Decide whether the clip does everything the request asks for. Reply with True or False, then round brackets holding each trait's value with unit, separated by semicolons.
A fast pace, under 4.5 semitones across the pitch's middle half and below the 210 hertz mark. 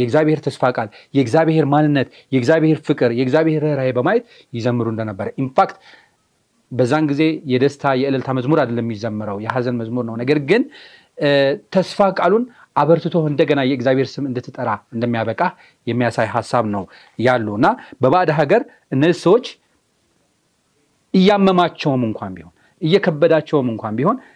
False (120 wpm; 4.8 semitones; 140 Hz)